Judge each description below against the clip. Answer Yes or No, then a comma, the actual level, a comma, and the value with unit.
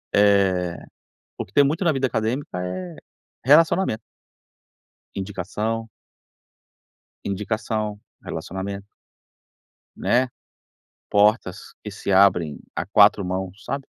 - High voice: No, low, 105 Hz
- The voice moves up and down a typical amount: Yes, average, 3.2 semitones